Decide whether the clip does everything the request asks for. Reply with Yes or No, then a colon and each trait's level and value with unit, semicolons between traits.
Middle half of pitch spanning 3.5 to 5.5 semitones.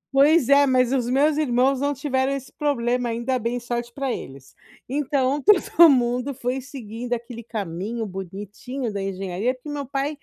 No: average, 3.0 semitones